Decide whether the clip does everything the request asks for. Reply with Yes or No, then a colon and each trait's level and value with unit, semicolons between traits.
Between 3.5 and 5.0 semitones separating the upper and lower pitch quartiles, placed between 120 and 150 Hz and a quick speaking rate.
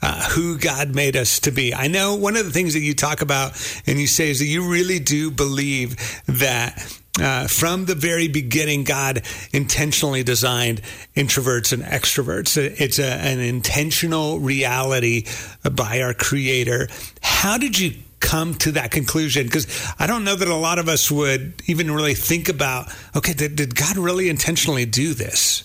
No: average, 4.2 semitones; medium, 140 Hz; average, 175 wpm